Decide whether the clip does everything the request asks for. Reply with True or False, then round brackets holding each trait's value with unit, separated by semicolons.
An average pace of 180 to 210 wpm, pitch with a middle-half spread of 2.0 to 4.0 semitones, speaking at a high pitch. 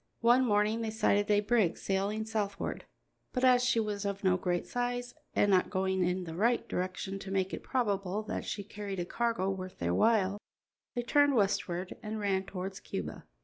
True (190 wpm; 3.0 semitones; 205 Hz)